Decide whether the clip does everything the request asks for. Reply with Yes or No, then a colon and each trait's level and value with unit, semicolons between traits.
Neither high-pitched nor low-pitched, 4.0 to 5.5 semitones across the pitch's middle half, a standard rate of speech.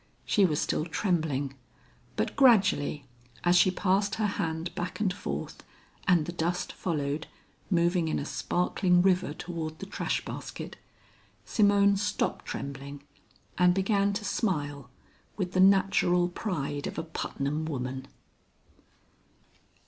No: medium, 175 Hz; average, 4.4 semitones; slow, 125 wpm